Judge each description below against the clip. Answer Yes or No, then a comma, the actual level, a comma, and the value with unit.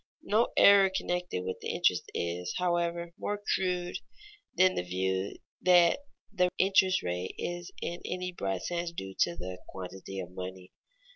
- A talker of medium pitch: Yes, medium, 170 Hz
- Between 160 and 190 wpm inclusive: No, average, 145 wpm